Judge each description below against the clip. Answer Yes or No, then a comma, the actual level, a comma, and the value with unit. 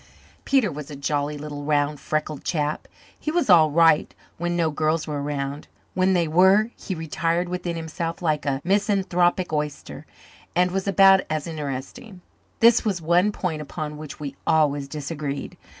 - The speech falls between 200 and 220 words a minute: No, average, 165 wpm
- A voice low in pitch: No, medium, 160 Hz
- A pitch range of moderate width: Yes, average, 3.4 semitones